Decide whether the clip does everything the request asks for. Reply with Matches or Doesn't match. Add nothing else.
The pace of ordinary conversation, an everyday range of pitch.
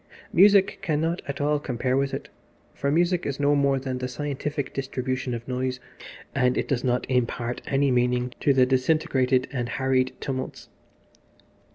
Doesn't match